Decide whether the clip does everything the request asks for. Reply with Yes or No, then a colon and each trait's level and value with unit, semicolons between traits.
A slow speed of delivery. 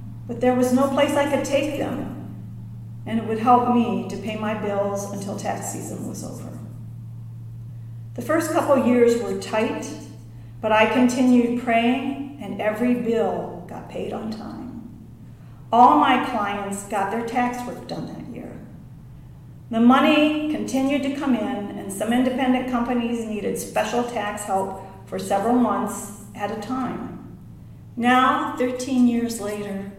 No: average, 150 wpm